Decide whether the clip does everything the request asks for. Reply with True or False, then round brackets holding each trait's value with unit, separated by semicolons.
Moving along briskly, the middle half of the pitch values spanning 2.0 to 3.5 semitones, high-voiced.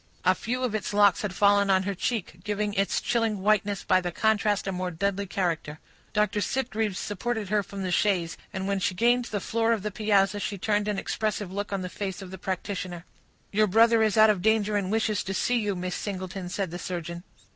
True (220 wpm; 2.4 semitones; 200 Hz)